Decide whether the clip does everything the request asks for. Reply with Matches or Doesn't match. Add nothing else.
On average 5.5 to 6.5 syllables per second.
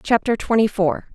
Doesn't match